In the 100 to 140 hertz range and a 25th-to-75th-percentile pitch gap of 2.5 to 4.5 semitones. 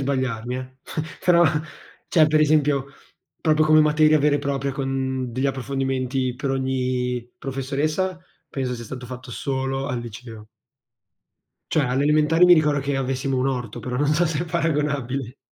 Yes: low, 135 Hz; average, 2.8 semitones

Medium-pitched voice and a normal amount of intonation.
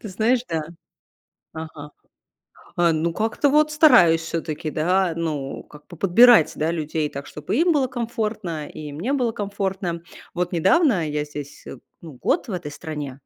No: medium, 170 Hz; wide, 6.3 semitones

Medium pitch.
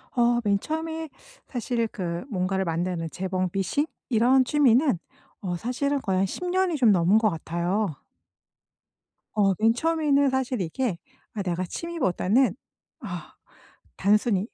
No: high, 215 Hz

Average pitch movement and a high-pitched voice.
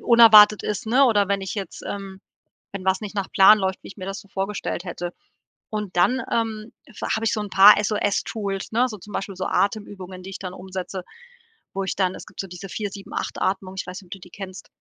No: narrow, 1.9 semitones; high, 195 Hz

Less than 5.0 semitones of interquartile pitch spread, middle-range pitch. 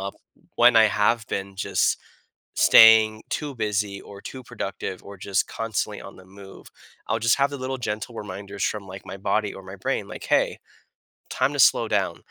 No: narrow, 2.6 semitones; low, 105 Hz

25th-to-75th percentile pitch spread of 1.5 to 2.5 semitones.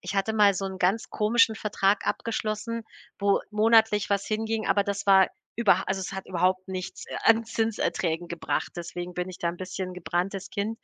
No: average, 2.9 semitones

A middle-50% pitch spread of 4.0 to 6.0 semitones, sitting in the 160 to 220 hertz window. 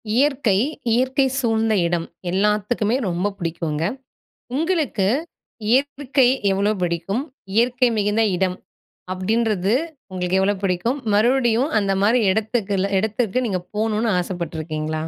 Yes: average, 4.5 semitones; high, 210 Hz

